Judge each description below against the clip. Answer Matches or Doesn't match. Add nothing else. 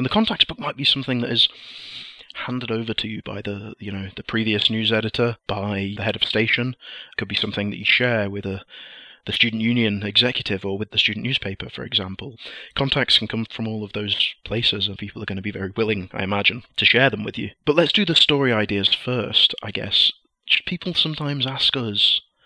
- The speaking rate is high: Matches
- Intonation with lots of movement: Doesn't match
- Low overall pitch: Matches